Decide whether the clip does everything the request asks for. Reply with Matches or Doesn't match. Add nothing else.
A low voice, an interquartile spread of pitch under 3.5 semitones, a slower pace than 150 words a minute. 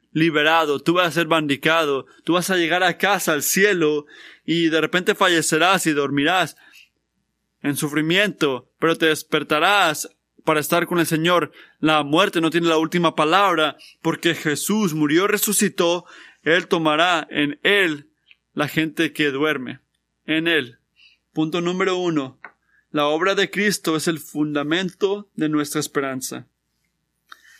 Doesn't match